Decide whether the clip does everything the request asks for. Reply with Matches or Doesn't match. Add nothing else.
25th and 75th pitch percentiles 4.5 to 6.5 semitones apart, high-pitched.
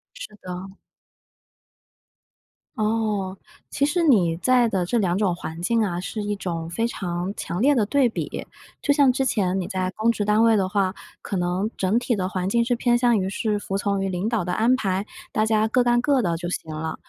Doesn't match